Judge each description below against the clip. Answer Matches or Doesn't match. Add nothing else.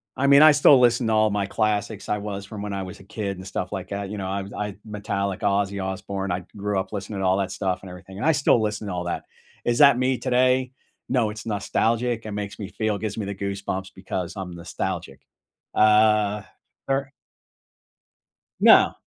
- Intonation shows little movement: Matches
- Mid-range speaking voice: Doesn't match